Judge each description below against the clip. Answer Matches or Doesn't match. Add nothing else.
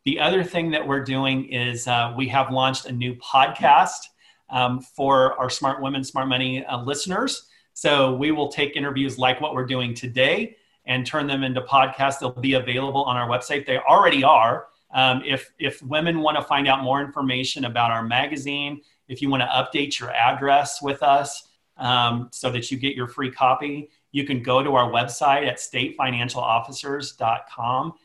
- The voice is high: Doesn't match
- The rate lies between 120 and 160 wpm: Doesn't match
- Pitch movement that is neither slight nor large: Doesn't match